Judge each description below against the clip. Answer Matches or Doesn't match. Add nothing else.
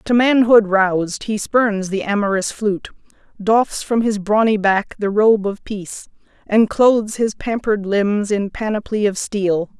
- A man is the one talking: Doesn't match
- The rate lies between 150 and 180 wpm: Matches